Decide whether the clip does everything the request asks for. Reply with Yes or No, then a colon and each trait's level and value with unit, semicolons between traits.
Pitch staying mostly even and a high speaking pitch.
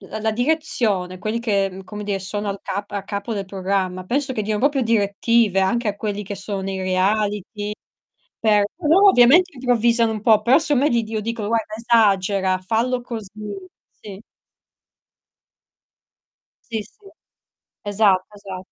No: average, 3.1 semitones; high, 210 Hz